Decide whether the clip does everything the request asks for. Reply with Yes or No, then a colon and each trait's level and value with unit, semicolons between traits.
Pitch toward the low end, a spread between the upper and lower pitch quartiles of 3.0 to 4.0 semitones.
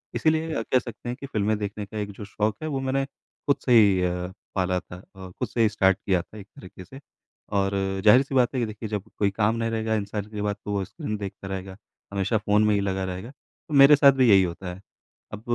Yes: low, 105 Hz; average, 3.6 semitones